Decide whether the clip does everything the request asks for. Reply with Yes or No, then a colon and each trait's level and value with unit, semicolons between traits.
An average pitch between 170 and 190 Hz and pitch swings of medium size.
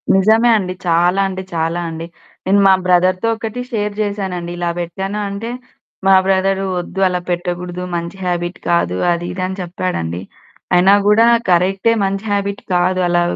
No: medium, 185 Hz; narrow, 2.1 semitones